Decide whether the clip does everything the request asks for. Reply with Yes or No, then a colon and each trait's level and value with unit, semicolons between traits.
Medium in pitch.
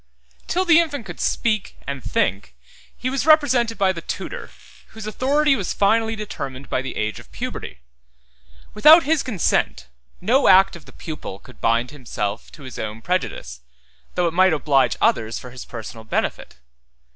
Yes: medium, 180 Hz